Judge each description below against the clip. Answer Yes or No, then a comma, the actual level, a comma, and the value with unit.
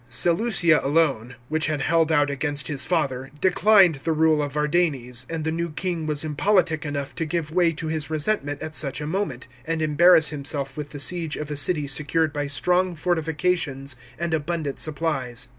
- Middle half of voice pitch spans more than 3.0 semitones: No, narrow, 2.6 semitones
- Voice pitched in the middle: Yes, medium, 155 Hz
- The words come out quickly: No, average, 180 wpm